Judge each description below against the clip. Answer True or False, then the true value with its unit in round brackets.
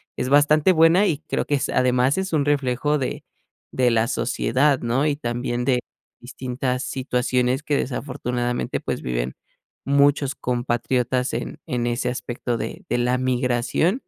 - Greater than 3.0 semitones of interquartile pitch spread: False (2.7 semitones)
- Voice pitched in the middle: False (125 Hz)